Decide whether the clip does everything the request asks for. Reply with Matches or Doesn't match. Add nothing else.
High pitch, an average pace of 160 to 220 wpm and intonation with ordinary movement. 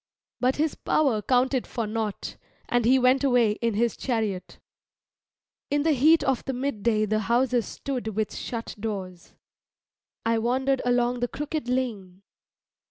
Doesn't match